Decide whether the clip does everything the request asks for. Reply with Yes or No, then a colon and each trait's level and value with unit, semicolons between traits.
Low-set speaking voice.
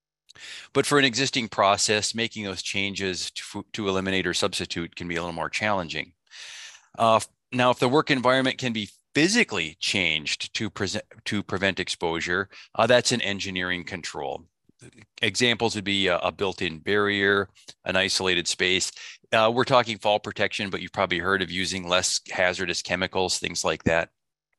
Yes: low, 100 Hz